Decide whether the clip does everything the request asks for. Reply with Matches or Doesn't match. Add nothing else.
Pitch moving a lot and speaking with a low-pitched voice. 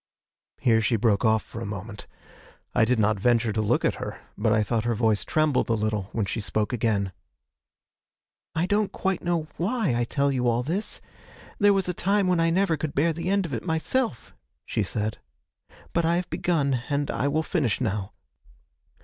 Matches